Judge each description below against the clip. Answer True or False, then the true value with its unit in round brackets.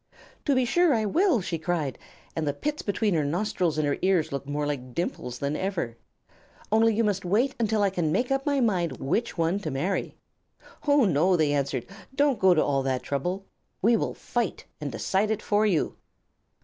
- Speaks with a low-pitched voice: False (185 Hz)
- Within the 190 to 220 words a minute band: True (200 wpm)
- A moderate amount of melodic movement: False (7.0 semitones)